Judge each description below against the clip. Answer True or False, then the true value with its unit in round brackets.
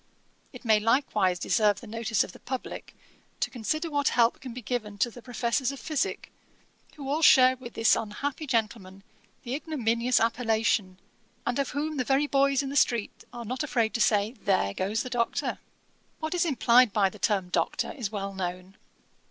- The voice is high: True (235 Hz)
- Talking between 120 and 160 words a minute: False (185 wpm)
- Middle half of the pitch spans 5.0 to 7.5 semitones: False (4.3 semitones)